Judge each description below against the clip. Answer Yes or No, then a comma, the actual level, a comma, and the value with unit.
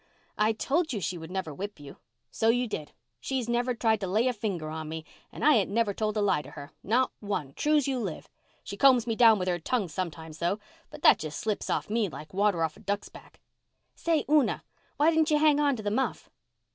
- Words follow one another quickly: Yes, fast, 230 wpm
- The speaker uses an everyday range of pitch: No, wide, 6.0 semitones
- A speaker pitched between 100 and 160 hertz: No, high, 215 Hz